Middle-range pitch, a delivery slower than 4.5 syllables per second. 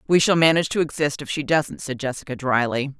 No: medium, 145 Hz; 6.1 syllables/s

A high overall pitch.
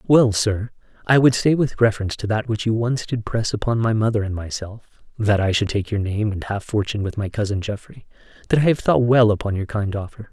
No: low, 110 Hz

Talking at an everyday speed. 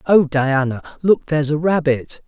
Yes: average, 160 wpm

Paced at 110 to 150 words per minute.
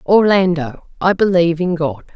Yes: average, 140 wpm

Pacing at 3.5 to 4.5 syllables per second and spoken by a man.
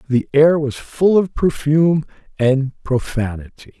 Yes: 4.0 syllables/s; male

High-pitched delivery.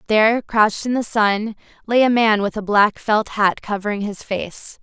Yes: high, 215 Hz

